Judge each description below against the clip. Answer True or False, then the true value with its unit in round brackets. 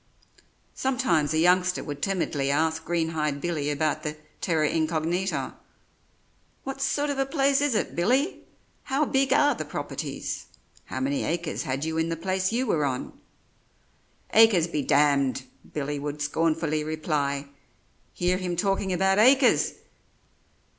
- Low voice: False (165 Hz)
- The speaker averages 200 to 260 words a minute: False (140 wpm)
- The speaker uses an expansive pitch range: True (5.9 semitones)